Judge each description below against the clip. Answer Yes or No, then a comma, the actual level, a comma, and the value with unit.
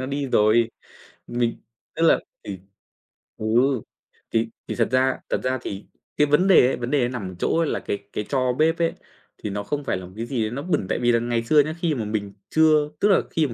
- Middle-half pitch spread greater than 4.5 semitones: Yes, average, 5.0 semitones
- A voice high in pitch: No, low, 125 Hz